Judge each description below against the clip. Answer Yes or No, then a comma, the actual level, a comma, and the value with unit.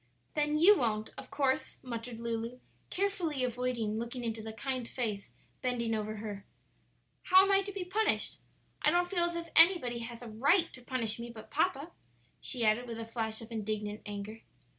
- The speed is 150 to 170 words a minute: No, average, 185 wpm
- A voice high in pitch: Yes, high, 240 Hz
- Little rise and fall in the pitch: No, wide, 5.5 semitones